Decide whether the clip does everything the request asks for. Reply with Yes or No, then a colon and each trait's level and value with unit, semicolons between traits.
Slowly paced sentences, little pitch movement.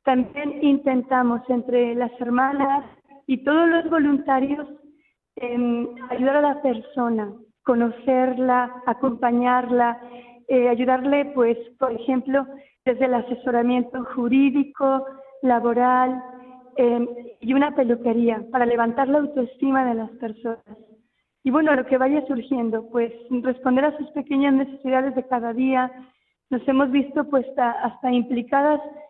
Yes: slow, 120 wpm; narrow, 2.1 semitones